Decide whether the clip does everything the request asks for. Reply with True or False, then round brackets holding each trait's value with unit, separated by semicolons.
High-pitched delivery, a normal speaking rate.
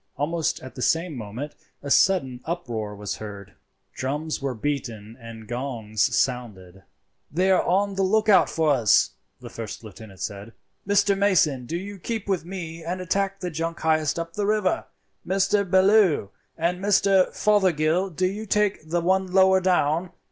False (165 Hz; 160 wpm)